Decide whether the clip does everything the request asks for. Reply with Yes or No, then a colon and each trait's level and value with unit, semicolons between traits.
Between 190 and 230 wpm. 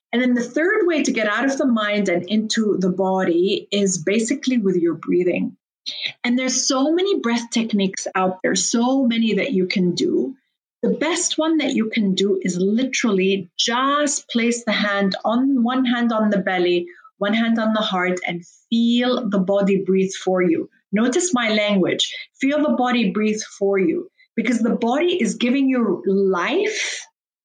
No: average, 175 wpm